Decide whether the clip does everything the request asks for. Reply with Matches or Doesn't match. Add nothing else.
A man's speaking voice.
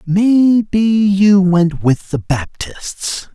Matches